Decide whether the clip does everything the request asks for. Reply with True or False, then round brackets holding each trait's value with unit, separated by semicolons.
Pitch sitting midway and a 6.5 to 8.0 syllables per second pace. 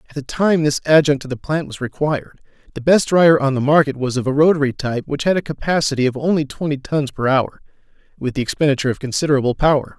True (145 Hz; 6.6 syllables/s)